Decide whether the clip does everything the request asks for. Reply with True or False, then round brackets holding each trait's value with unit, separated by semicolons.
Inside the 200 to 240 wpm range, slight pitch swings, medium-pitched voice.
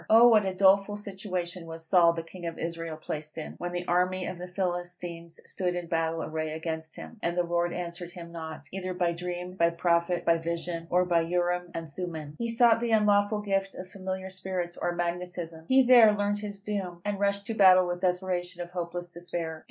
True (205 wpm; 2.1 semitones; 175 Hz)